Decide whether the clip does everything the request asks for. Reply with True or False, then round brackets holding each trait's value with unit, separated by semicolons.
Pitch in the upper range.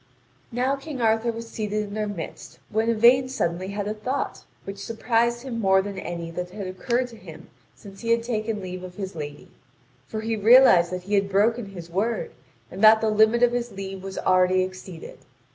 True (210 Hz)